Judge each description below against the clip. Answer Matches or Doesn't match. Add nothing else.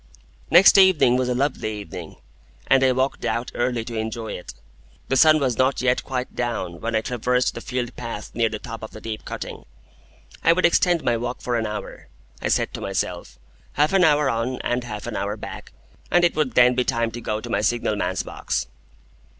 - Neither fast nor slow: Doesn't match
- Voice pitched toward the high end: Doesn't match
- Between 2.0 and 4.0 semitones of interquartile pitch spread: Matches